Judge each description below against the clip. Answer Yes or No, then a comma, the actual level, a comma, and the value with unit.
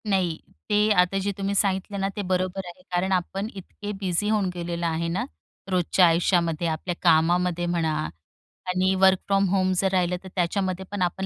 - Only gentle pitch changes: Yes, narrow, 1.9 semitones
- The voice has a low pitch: No, medium, 185 Hz